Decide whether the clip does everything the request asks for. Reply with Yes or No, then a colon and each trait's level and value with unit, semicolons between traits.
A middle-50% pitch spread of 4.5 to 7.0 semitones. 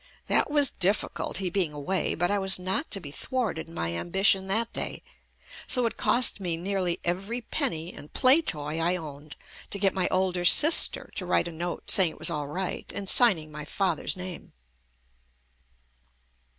No: average, 3.5 semitones